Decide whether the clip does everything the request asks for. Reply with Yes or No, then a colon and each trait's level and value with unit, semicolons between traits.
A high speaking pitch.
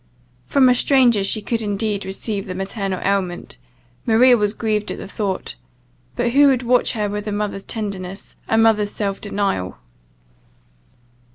Yes: high, 210 Hz